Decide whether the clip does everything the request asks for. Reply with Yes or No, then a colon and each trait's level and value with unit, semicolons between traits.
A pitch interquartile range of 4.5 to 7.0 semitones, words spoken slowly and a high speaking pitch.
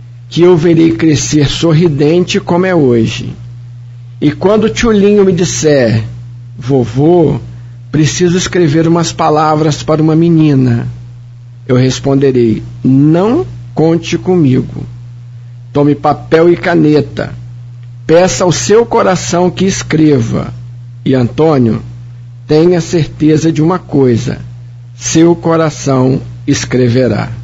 No: wide, 5.5 semitones; slow, 105 wpm; medium, 140 Hz